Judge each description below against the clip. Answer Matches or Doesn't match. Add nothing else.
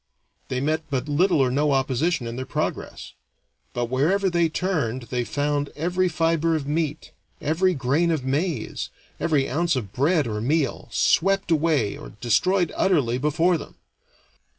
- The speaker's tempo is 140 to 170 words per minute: Matches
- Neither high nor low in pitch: Matches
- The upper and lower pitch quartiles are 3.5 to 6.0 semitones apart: Matches